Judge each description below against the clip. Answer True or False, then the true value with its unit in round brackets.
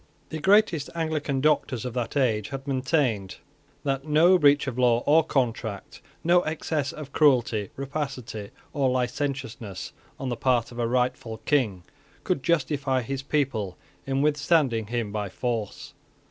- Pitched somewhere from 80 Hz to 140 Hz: True (135 Hz)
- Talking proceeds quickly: False (145 wpm)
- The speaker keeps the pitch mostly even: False (3.8 semitones)